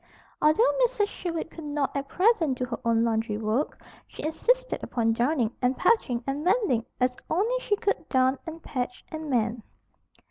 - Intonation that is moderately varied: No, wide, 6.3 semitones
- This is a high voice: Yes, very high, 275 Hz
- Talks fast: No, average, 170 wpm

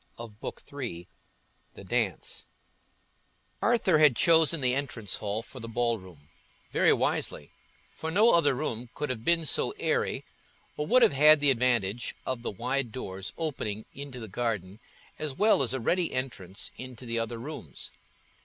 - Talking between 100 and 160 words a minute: Yes, average, 155 wpm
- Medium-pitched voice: No, low, 125 Hz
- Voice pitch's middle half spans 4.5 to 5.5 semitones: Yes, average, 5.0 semitones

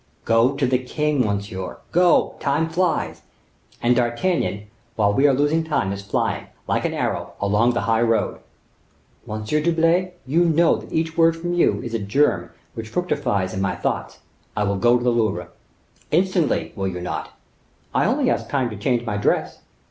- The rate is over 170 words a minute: Yes, average, 180 wpm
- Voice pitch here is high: No, low, 125 Hz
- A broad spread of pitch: Yes, wide, 7.6 semitones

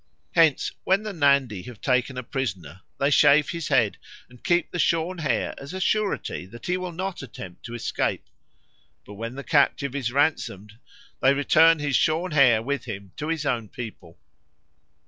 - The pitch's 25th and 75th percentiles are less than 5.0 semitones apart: No, wide, 5.5 semitones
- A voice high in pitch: No, medium, 140 Hz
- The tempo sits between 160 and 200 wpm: Yes, average, 175 wpm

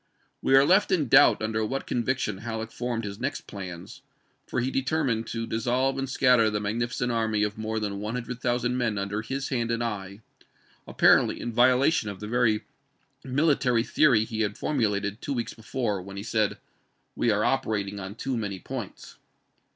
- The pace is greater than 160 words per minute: Yes, average, 185 wpm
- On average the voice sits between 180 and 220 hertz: No, low, 115 Hz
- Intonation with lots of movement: No, average, 3.1 semitones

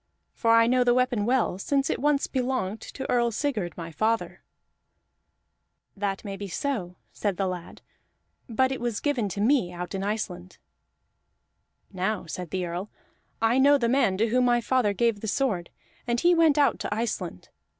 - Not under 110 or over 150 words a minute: No, average, 170 wpm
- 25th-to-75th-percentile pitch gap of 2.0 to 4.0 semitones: No, average, 5.0 semitones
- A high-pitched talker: Yes, high, 225 Hz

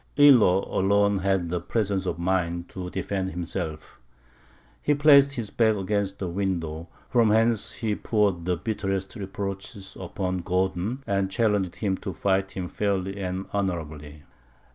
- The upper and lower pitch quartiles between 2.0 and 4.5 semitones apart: Yes, narrow, 2.4 semitones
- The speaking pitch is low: Yes, very low, 95 Hz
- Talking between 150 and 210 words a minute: No, average, 140 wpm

